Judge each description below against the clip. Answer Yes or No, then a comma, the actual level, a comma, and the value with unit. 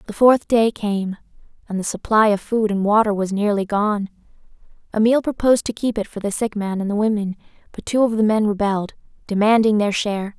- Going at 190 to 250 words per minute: Yes, average, 200 wpm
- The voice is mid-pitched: No, high, 210 Hz